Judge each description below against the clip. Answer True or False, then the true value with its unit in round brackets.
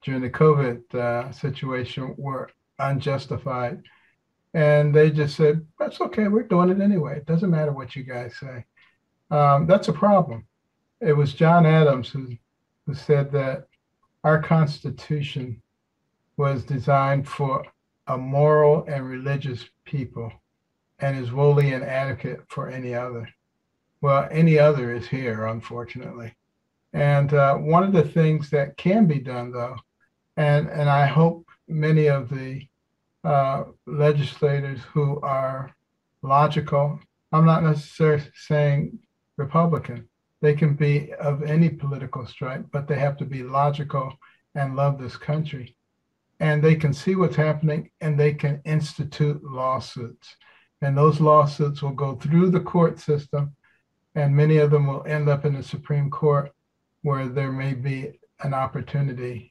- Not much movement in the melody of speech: True (2.3 semitones)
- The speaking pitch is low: False (145 Hz)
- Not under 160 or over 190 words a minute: False (140 wpm)